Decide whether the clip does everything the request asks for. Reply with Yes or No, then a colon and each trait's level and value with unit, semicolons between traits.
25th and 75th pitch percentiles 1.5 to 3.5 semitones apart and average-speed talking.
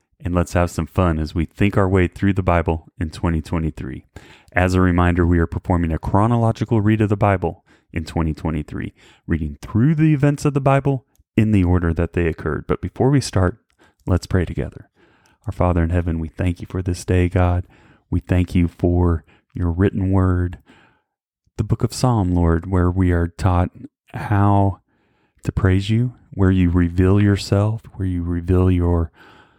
Yes: average, 2.8 semitones; average, 180 wpm